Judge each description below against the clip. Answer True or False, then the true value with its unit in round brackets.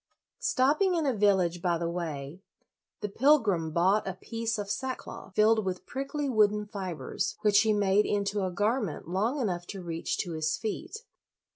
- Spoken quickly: False (165 wpm)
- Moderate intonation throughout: True (4.2 semitones)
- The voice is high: True (205 Hz)